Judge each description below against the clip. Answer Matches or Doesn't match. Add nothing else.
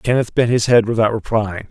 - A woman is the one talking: Doesn't match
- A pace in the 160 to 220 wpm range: Matches